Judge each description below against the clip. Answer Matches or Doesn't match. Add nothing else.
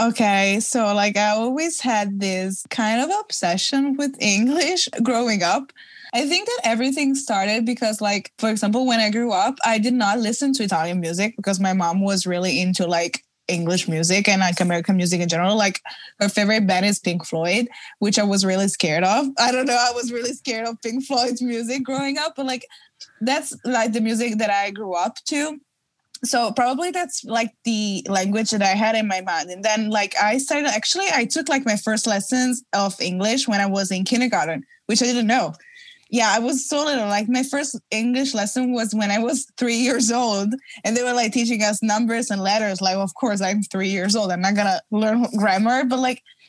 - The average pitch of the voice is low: Doesn't match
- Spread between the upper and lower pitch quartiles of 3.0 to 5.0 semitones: Matches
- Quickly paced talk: Matches